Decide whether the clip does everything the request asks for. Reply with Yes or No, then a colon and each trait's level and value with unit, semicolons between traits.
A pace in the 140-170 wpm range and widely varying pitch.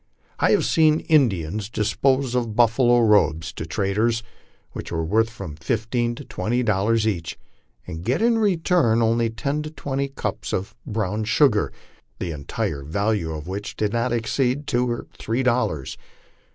No: average, 165 wpm; average, 4.3 semitones